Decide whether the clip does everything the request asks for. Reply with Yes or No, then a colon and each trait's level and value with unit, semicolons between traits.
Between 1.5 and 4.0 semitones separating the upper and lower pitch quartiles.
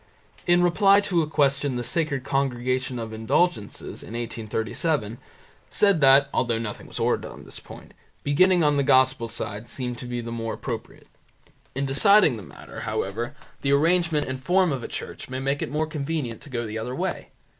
No: average, 4.7 semitones